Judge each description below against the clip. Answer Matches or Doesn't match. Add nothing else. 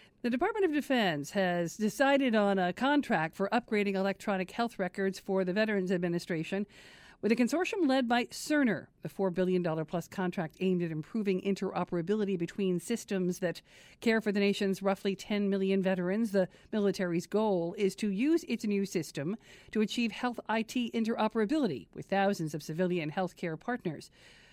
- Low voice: Doesn't match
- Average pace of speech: Matches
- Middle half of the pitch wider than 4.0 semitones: Doesn't match